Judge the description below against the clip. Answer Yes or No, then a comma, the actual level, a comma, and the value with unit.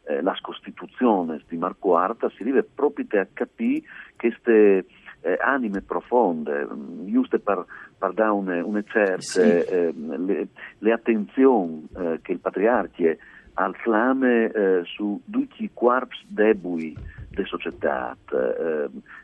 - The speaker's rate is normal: Yes, average, 125 wpm